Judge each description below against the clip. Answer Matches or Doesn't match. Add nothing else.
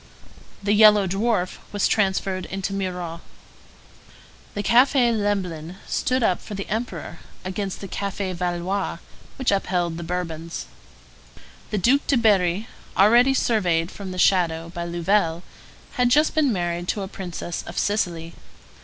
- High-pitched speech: Matches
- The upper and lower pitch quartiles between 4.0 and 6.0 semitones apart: Doesn't match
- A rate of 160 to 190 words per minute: Doesn't match